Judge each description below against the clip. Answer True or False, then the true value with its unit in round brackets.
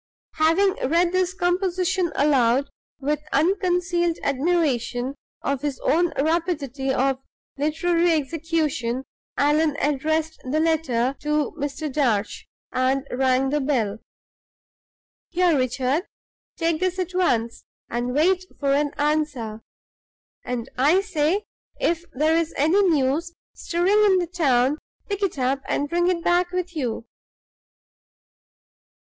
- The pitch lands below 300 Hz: False (305 Hz)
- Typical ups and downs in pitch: True (4.5 semitones)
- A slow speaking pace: True (115 wpm)